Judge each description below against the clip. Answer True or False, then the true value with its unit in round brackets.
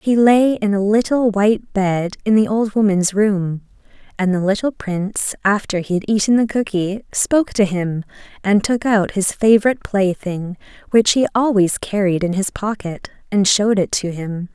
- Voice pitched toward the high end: True (205 Hz)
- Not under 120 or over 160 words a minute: False (175 wpm)